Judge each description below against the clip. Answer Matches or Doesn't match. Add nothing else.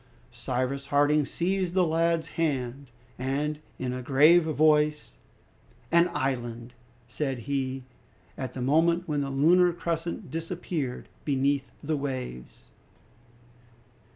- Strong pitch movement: Doesn't match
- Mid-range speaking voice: Matches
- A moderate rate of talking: Doesn't match